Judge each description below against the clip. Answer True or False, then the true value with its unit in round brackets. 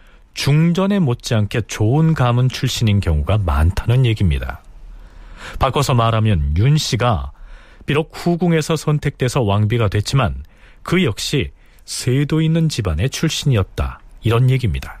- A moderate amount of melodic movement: False (6.4 semitones)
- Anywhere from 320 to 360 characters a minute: False (290 characters per minute)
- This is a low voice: True (120 Hz)